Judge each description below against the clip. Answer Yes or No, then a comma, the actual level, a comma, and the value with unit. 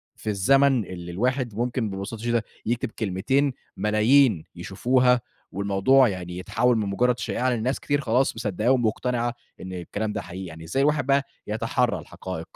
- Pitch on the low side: Yes, low, 115 Hz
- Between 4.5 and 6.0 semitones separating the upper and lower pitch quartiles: Yes, average, 4.8 semitones